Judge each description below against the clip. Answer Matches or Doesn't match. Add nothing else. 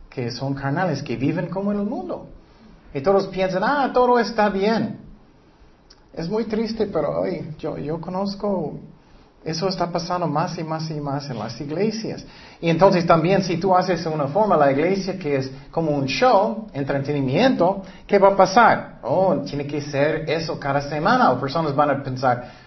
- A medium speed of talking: Matches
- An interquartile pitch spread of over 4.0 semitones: Matches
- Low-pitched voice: Doesn't match